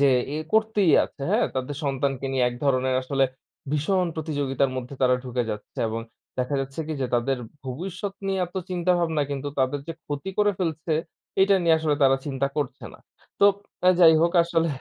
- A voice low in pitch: No, medium, 145 Hz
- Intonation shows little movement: No, average, 4.4 semitones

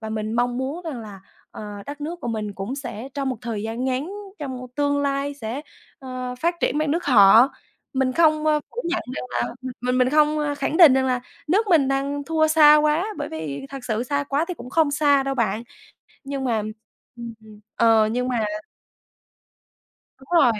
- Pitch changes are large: No, average, 3.8 semitones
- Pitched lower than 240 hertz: No, very high, 270 Hz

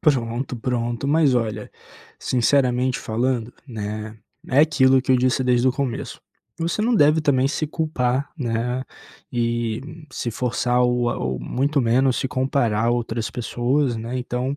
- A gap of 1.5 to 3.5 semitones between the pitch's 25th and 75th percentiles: Yes, narrow, 2.5 semitones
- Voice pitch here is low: Yes, low, 125 Hz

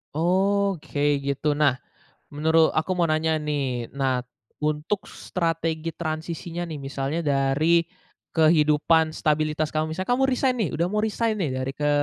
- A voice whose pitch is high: No, medium, 155 Hz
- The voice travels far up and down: No, narrow, 2.6 semitones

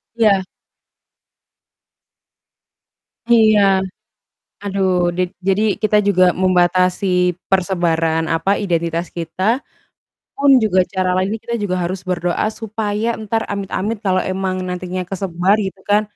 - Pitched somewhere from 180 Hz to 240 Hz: Yes, high, 190 Hz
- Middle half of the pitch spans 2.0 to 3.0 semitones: Yes, narrow, 2.4 semitones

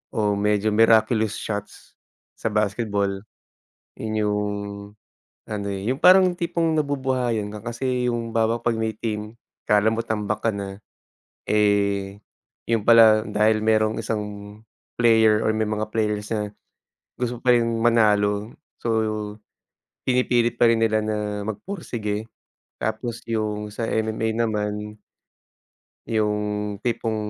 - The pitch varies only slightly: Yes, narrow, 1.6 semitones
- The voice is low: Yes, low, 110 Hz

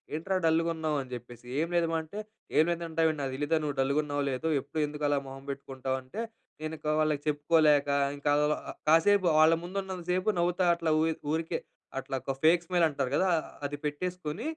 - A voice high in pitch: No, medium, 155 Hz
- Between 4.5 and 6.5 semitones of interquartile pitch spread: No, average, 2.7 semitones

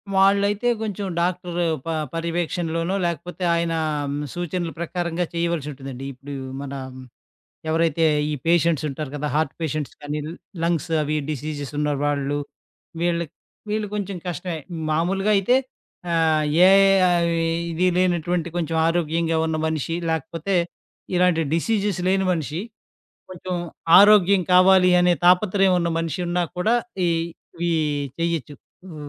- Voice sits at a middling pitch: Yes, medium, 170 Hz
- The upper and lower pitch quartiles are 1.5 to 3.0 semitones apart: Yes, narrow, 2.5 semitones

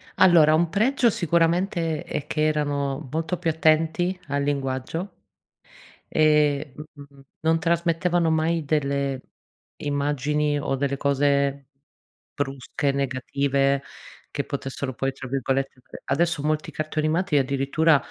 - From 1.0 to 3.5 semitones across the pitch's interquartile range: Yes, average, 2.7 semitones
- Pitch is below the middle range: No, medium, 150 Hz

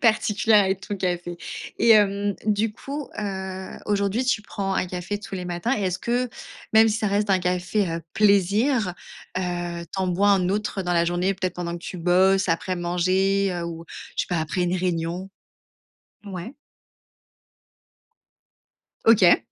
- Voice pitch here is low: No, high, 190 Hz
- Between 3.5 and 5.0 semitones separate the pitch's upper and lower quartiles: No, average, 2.7 semitones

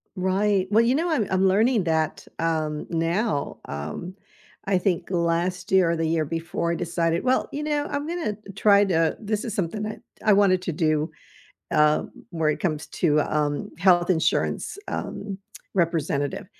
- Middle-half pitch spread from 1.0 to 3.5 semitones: No, average, 4.0 semitones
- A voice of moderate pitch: Yes, medium, 175 Hz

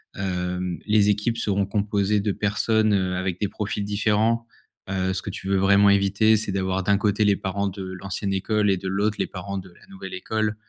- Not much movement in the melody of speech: Yes, narrow, 1.7 semitones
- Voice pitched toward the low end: Yes, low, 100 Hz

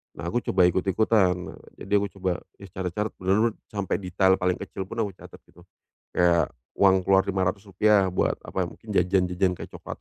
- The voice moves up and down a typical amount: No, narrow, 1.9 semitones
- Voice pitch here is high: No, very low, 95 Hz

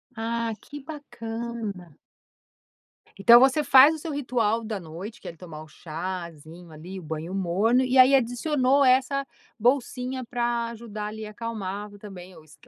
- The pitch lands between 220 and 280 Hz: Yes, high, 225 Hz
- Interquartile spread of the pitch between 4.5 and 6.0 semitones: Yes, wide, 5.5 semitones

